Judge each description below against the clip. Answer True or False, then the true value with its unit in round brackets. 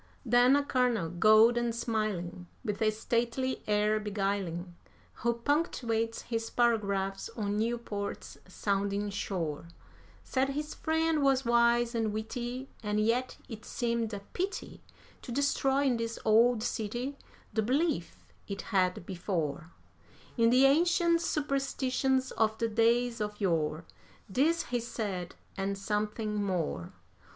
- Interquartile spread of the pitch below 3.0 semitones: False (3.7 semitones)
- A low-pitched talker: False (225 Hz)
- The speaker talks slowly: True (125 wpm)